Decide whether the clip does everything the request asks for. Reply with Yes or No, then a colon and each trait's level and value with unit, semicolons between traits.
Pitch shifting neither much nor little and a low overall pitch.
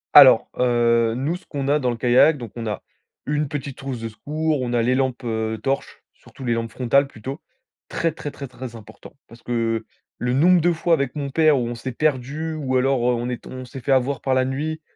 Yes: average, 3.3 semitones; low, 130 Hz